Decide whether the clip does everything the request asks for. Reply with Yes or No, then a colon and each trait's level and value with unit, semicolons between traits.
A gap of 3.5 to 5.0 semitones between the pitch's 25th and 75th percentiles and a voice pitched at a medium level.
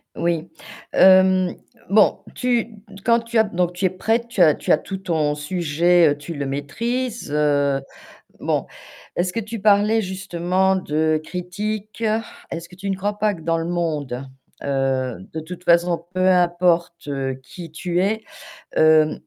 Yes: average, 4.0 semitones; medium, 175 Hz